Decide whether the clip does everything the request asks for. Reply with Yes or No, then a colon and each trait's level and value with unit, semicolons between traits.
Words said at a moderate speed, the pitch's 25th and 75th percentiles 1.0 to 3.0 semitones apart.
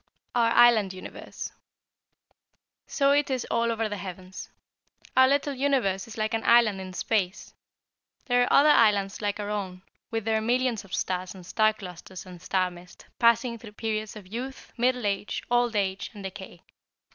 No: average, 170 wpm; average, 3.9 semitones